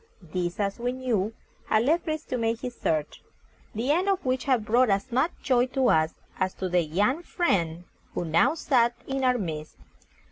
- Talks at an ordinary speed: Yes, average, 190 wpm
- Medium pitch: No, high, 235 Hz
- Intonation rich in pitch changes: Yes, wide, 5.8 semitones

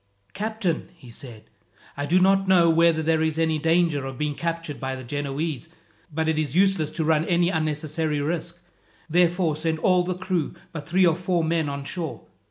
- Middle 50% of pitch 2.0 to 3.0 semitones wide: Yes, narrow, 2.6 semitones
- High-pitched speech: No, medium, 160 Hz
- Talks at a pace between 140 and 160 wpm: No, average, 185 wpm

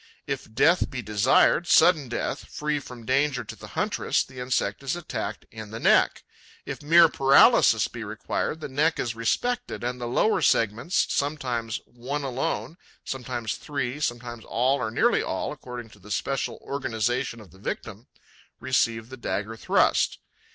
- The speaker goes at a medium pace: Yes, average, 160 wpm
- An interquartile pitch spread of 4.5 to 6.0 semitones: No, average, 3.8 semitones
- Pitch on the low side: Yes, low, 125 Hz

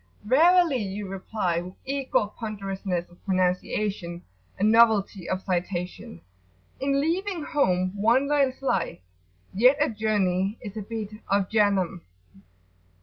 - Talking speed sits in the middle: No, slow, 120 wpm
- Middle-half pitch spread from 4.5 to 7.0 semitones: Yes, wide, 5.4 semitones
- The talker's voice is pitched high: Yes, high, 205 Hz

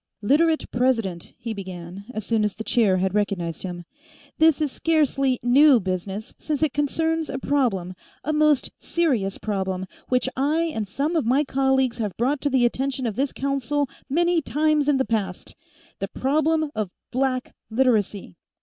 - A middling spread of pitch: No, wide, 6.0 semitones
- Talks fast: No, average, 165 wpm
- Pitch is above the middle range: Yes, very high, 260 Hz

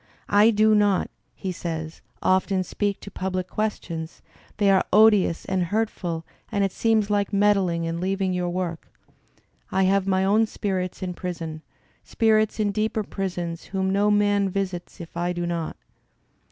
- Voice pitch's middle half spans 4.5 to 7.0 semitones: No, average, 2.7 semitones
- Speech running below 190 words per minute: Yes, average, 155 wpm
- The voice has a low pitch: No, high, 190 Hz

